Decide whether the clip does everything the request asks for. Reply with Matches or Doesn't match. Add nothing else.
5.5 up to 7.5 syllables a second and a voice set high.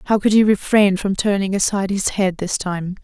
Doesn't match